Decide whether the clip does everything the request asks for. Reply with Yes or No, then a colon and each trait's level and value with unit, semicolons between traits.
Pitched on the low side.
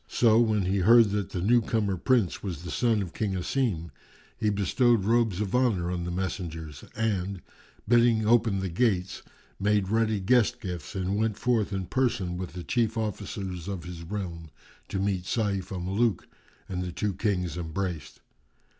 Yes: low, 100 Hz